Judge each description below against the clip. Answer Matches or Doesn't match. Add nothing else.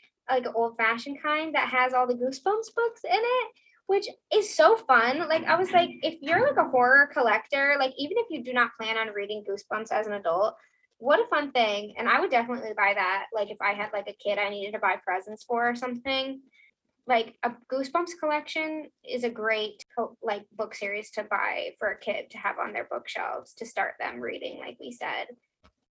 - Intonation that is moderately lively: Doesn't match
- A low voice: Doesn't match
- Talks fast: Matches